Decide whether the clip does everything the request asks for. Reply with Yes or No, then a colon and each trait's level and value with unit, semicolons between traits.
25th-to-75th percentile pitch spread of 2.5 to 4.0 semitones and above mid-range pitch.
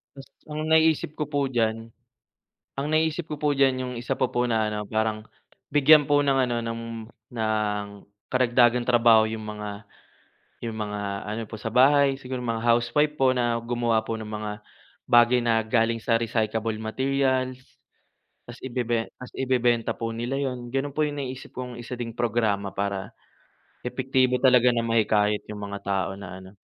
No: average, 3.0 semitones; low, 120 Hz